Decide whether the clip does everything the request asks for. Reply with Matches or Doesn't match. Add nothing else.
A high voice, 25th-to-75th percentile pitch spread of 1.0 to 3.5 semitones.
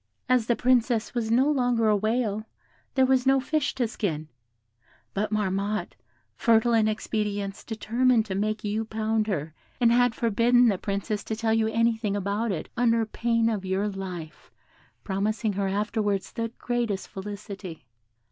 Matches